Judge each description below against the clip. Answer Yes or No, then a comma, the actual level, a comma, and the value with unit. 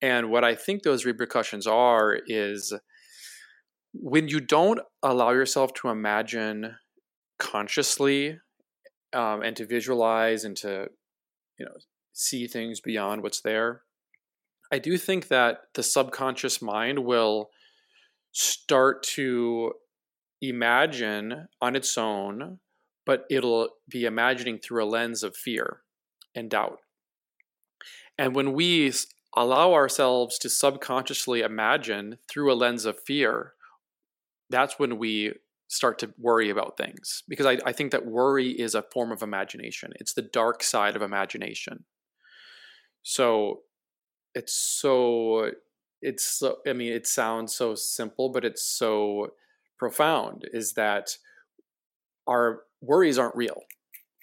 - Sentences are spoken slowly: Yes, slow, 125 wpm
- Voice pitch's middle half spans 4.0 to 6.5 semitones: No, average, 3.4 semitones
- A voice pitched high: No, low, 120 Hz